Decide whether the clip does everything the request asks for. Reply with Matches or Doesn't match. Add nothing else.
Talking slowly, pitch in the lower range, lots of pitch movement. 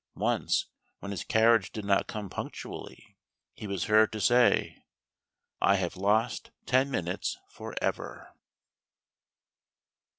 Doesn't match